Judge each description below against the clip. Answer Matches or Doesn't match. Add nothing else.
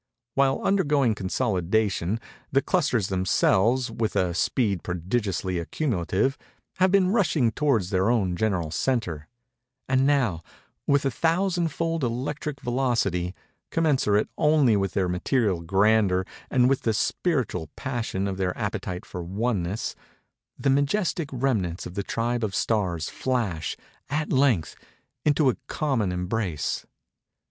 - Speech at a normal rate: Doesn't match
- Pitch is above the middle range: Doesn't match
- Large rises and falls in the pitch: Matches